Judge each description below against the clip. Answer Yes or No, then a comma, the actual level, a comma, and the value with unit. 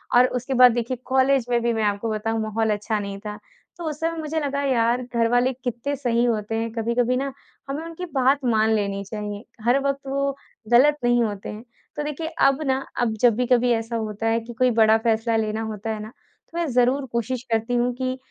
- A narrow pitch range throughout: No, average, 3.0 semitones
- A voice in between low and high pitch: No, high, 240 Hz